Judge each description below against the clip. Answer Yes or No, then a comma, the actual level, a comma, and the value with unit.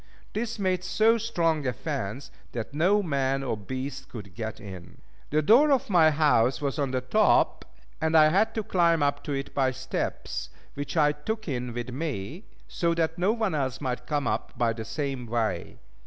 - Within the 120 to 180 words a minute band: No, average, 190 wpm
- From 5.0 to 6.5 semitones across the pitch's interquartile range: Yes, average, 5.3 semitones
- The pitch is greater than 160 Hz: No, medium, 145 Hz